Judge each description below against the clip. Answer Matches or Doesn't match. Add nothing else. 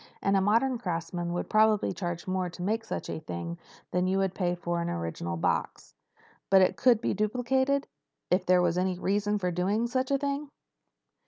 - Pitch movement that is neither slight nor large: Matches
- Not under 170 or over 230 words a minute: Matches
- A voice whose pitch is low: Doesn't match